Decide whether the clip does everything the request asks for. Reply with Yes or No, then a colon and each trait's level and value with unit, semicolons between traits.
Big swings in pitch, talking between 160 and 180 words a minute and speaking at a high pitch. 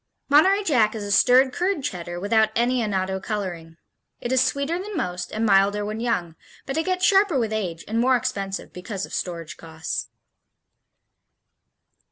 Yes: wide, 5.9 semitones; average, 165 wpm; high, 220 Hz